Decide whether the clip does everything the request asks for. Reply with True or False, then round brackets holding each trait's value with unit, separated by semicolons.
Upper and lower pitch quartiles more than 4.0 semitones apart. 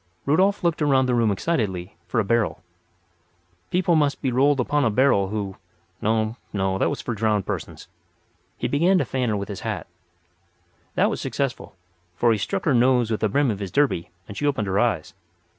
True (5.6 semitones)